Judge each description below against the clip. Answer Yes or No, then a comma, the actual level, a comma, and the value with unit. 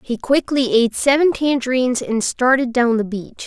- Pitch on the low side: No, very high, 250 Hz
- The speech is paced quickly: No, average, 175 wpm